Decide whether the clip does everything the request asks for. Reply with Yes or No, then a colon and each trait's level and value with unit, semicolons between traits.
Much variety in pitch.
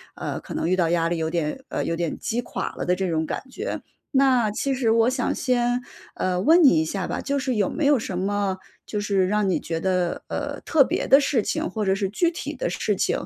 Yes: wide, 6.2 semitones